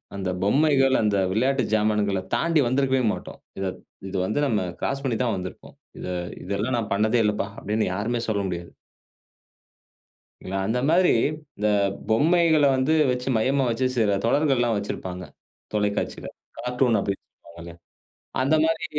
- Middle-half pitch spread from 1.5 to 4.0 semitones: No, average, 4.7 semitones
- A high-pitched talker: No, low, 115 Hz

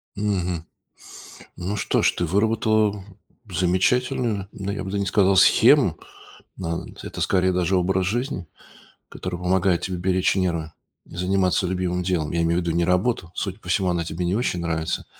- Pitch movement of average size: No, narrow, 2.1 semitones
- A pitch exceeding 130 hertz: No, very low, 90 Hz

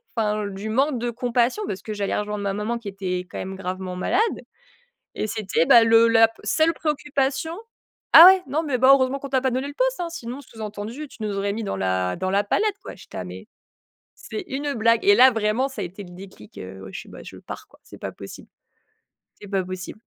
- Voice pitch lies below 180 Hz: No, high, 225 Hz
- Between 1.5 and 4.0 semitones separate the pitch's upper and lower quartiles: No, average, 5.3 semitones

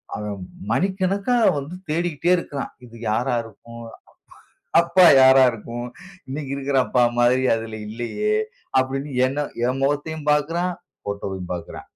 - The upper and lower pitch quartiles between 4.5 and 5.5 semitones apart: Yes, average, 5.2 semitones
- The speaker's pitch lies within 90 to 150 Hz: Yes, low, 135 Hz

